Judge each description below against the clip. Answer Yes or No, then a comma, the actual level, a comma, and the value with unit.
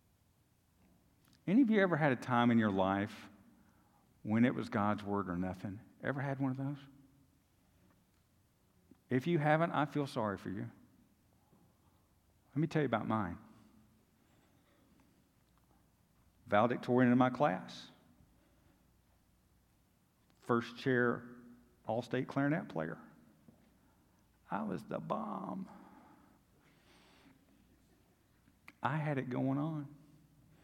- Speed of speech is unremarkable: No, slow, 105 wpm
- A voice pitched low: Yes, low, 120 Hz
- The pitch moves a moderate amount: No, wide, 6.2 semitones